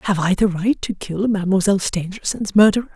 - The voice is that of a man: No, female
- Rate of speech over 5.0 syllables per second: Yes, 6.3 syllables/s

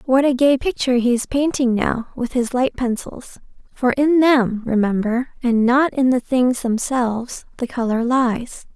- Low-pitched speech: No, very high, 250 Hz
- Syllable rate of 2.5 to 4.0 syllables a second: No, 4.4 syllables/s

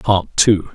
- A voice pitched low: Yes, low, 100 Hz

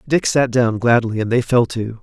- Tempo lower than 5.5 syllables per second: Yes, 4.8 syllables/s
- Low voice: Yes, low, 120 Hz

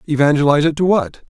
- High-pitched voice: No, medium, 150 Hz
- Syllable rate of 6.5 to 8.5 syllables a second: Yes, 7.0 syllables/s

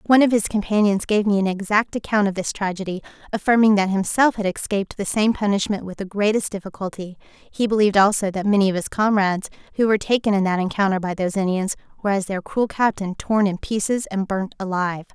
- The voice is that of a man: No, female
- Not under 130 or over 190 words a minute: No, fast, 205 wpm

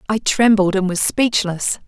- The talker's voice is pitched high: Yes, high, 205 Hz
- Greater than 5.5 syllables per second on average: No, 4.3 syllables/s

